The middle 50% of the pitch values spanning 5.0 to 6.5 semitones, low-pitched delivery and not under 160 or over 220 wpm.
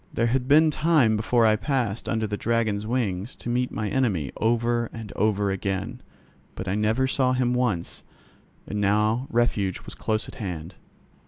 No: average, 3.2 semitones; low, 110 Hz; average, 170 wpm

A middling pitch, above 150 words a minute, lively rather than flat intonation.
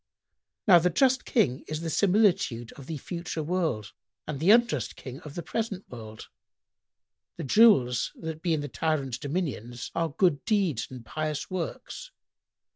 Yes: medium, 160 Hz; average, 165 wpm; wide, 5.8 semitones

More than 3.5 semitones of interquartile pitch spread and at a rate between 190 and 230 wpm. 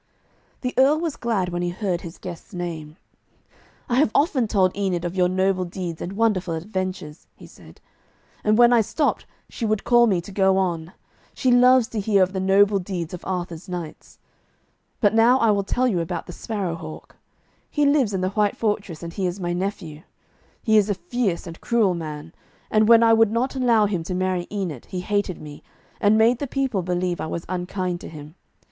Yes: average, 4.1 semitones; fast, 205 wpm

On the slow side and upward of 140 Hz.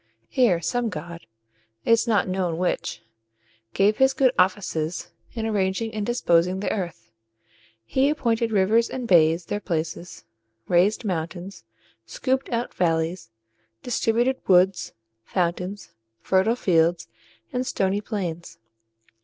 Yes: slow, 120 wpm; high, 190 Hz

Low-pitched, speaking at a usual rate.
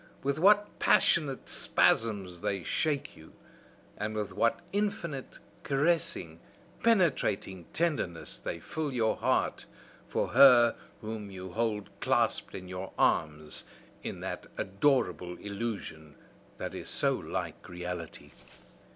No: low, 105 Hz; slow, 115 wpm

